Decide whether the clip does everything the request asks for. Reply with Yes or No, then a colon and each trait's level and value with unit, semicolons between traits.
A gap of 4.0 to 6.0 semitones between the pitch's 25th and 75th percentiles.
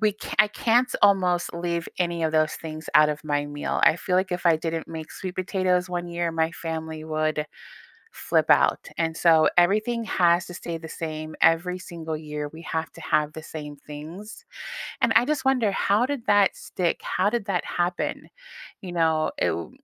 No: average, 2.9 semitones